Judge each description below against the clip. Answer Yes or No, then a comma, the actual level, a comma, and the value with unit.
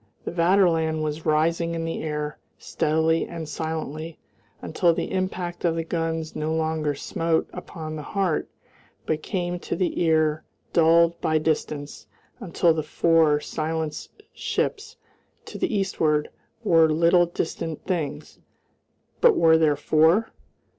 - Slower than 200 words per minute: Yes, slow, 135 wpm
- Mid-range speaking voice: Yes, medium, 160 Hz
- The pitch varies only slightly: Yes, narrow, 1.6 semitones